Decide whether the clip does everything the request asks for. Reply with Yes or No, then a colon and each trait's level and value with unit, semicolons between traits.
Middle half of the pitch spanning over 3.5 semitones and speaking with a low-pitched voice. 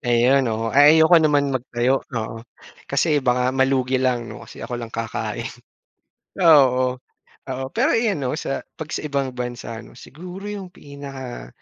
No: average, 2.9 semitones; low, 130 Hz